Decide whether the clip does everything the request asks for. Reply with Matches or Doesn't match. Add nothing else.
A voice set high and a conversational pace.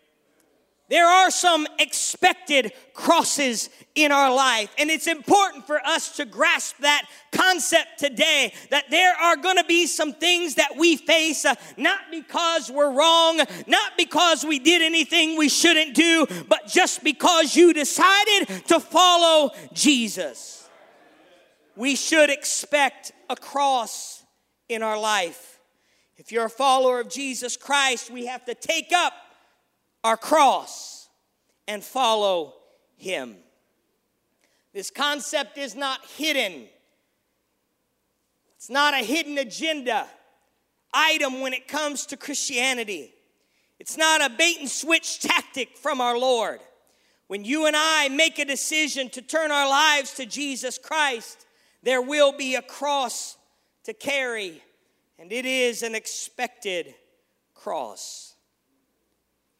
Doesn't match